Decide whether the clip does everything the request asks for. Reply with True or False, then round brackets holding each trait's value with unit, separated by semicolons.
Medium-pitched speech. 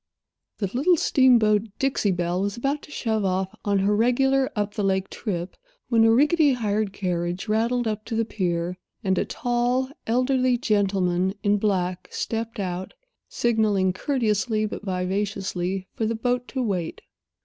False (210 Hz)